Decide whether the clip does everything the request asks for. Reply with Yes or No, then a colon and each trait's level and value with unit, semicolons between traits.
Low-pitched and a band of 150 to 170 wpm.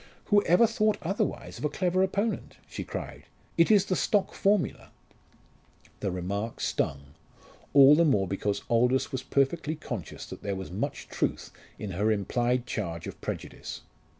Yes: low, 130 Hz; average, 155 wpm